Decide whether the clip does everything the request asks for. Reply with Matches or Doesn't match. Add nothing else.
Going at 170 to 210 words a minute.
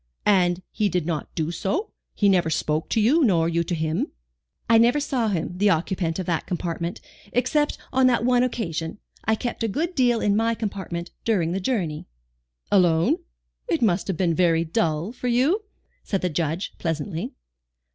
Matches